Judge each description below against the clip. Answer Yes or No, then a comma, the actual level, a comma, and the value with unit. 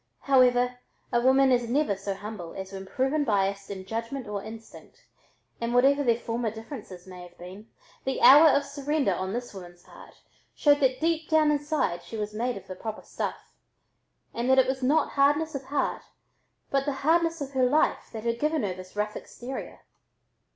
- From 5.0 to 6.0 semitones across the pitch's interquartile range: Yes, average, 5.3 semitones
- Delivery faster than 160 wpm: Yes, average, 185 wpm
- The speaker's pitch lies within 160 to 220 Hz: No, high, 245 Hz